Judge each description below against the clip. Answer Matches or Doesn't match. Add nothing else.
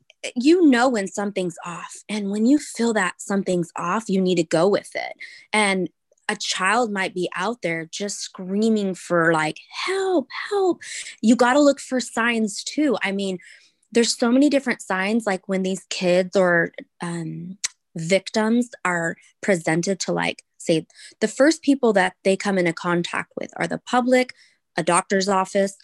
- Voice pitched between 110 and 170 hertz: Doesn't match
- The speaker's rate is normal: Matches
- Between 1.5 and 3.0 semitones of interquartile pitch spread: Doesn't match